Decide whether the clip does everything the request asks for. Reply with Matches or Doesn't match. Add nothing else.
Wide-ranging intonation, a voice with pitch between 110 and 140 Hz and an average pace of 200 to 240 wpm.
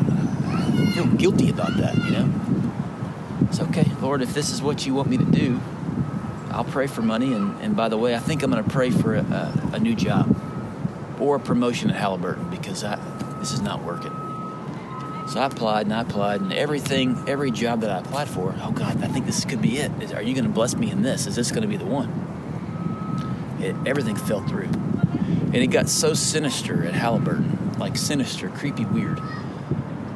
Matches